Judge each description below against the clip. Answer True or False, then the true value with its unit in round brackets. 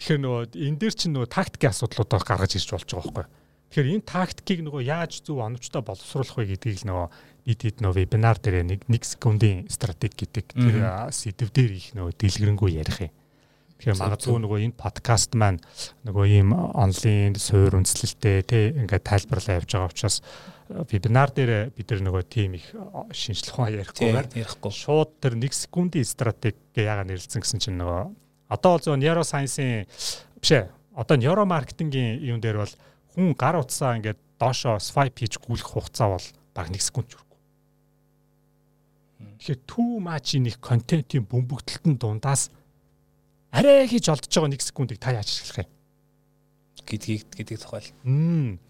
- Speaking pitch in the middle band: False (120 Hz)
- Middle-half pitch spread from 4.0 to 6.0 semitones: True (5.6 semitones)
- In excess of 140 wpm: True (155 wpm)